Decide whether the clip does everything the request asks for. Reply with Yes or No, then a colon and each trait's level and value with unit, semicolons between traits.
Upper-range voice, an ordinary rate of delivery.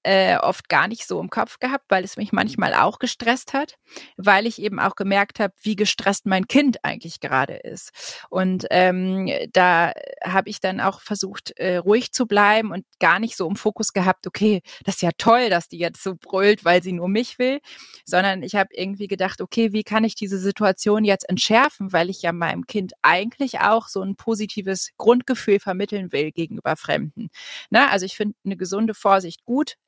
No: high, 200 Hz; fast, 195 wpm